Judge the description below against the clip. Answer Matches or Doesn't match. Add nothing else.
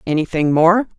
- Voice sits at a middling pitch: Matches